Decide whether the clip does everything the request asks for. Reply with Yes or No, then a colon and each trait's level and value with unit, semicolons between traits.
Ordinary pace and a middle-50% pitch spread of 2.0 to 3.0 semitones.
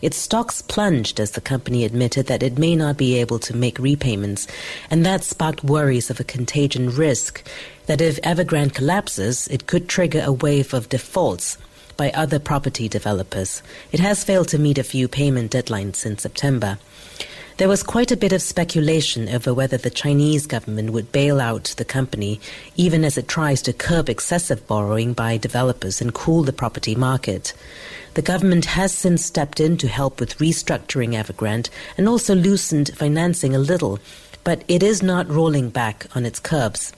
No: average, 175 wpm; wide, 5.4 semitones